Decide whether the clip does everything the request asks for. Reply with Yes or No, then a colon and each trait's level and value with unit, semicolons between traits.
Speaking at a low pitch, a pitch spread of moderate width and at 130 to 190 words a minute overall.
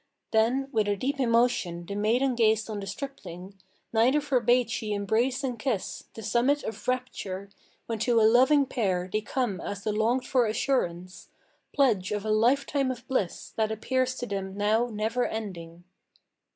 No: high, 225 Hz; average, 3.8 semitones; average, 165 wpm